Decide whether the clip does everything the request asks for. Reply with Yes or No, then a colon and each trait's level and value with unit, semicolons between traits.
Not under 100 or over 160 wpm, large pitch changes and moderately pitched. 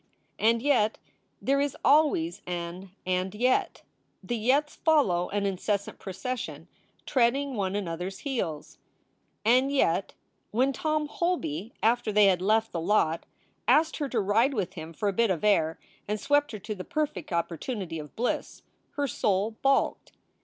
No: average, 155 wpm; wide, 6.6 semitones; high, 215 Hz